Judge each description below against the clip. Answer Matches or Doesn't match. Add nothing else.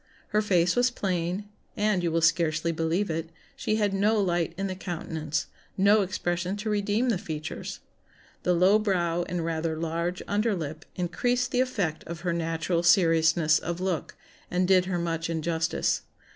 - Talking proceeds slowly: Doesn't match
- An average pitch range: Matches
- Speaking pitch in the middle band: Matches